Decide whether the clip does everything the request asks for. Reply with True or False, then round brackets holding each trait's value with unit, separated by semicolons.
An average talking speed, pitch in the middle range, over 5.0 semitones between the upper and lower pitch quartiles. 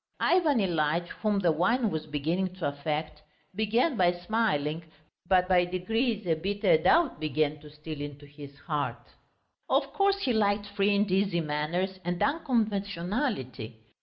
True (145 wpm; 180 Hz; 5.5 semitones)